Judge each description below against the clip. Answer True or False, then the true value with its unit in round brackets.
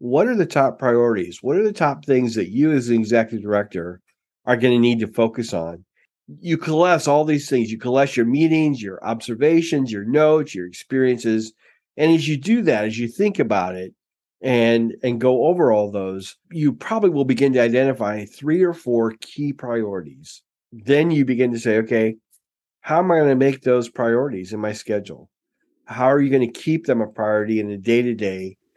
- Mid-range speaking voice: False (120 Hz)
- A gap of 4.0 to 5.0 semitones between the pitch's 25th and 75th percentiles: True (4.7 semitones)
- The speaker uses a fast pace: False (195 wpm)